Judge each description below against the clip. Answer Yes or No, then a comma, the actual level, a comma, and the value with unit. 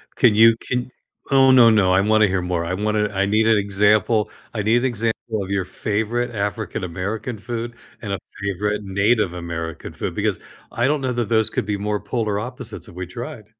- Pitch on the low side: Yes, low, 105 Hz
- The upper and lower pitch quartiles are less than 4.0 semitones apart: Yes, average, 2.8 semitones